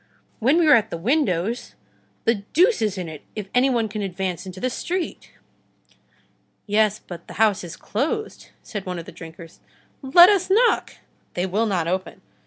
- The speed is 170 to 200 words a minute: Yes, average, 180 wpm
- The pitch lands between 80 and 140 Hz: No, high, 215 Hz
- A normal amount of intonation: No, wide, 6.6 semitones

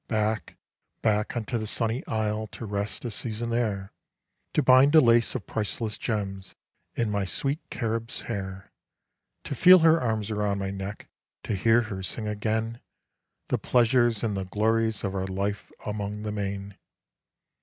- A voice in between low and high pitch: No, low, 110 Hz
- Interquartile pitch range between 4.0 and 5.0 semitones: No, narrow, 2.5 semitones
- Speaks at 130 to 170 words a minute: Yes, average, 155 wpm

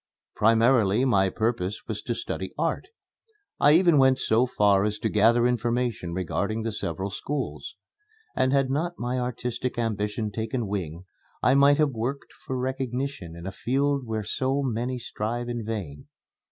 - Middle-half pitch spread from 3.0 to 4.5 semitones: Yes, average, 3.8 semitones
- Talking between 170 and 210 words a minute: No, average, 155 wpm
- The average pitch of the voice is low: Yes, low, 120 Hz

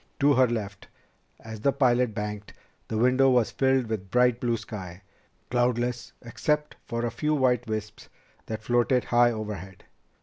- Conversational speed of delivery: Yes, average, 155 wpm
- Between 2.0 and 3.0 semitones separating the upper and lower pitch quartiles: Yes, narrow, 2.6 semitones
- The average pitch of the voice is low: Yes, low, 120 Hz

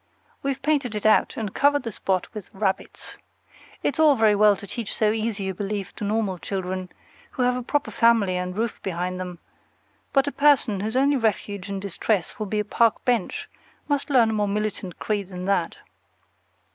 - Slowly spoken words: No, average, 190 wpm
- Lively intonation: No, average, 3.6 semitones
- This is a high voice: Yes, high, 210 Hz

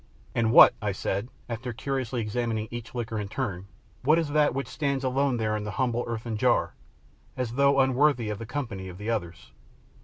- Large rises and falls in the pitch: No, average, 3.7 semitones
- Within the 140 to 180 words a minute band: No, average, 190 wpm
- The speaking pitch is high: No, low, 120 Hz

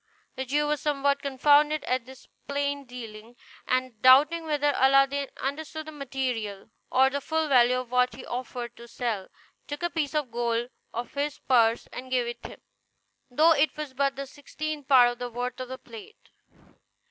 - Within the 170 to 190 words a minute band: Yes, average, 180 wpm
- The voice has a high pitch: Yes, very high, 265 Hz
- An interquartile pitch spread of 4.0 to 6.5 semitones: No, average, 2.9 semitones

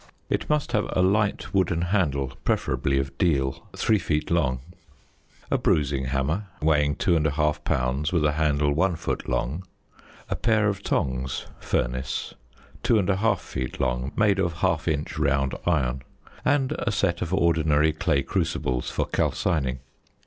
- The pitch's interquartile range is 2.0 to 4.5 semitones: No, wide, 5.4 semitones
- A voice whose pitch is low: Yes, very low, 80 Hz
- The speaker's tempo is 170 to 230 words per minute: No, average, 150 wpm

